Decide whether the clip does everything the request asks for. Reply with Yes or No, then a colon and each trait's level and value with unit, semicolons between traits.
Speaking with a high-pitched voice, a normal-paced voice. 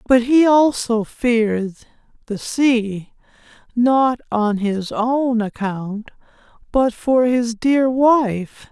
No: high, 235 Hz; slow, 110 wpm